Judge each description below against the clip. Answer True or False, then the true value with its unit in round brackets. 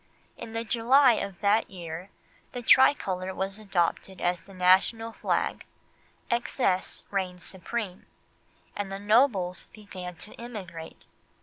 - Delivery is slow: True (120 wpm)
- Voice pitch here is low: False (195 Hz)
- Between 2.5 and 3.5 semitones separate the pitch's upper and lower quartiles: False (3.9 semitones)